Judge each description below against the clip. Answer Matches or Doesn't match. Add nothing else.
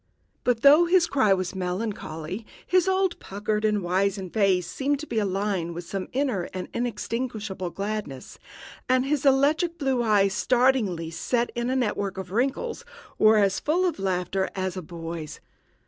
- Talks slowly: Doesn't match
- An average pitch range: Doesn't match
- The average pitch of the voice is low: Doesn't match